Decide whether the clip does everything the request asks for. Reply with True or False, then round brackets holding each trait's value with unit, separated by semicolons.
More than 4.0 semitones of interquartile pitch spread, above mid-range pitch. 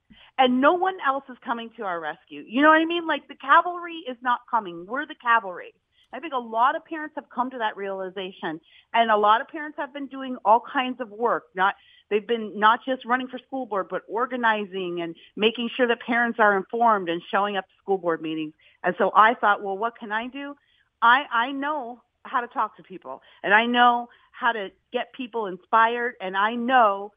True (4.4 semitones; 235 Hz)